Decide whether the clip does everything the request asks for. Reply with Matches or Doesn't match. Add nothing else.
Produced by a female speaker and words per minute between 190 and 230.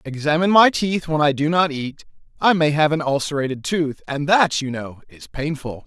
Doesn't match